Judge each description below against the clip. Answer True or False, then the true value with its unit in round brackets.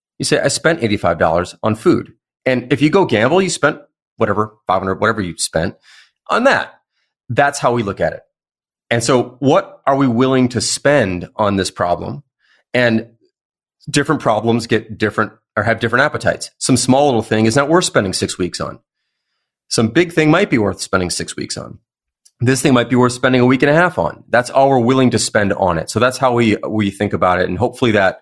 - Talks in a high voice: False (120 Hz)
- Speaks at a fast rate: True (210 wpm)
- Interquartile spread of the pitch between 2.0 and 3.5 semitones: False (4.2 semitones)